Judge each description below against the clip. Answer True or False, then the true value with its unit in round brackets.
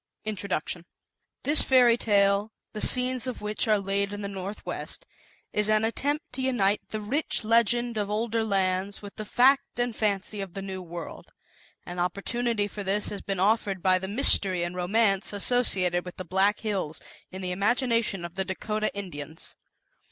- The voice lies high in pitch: True (205 Hz)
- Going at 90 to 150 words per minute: False (170 wpm)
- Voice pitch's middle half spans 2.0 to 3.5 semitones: True (3.2 semitones)